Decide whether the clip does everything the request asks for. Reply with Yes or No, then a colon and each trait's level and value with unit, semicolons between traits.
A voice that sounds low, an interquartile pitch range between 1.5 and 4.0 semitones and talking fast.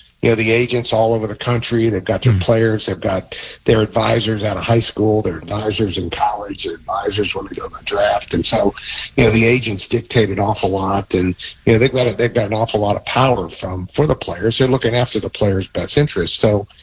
Yes: low, 110 Hz; average, 2.9 semitones; fast, 240 wpm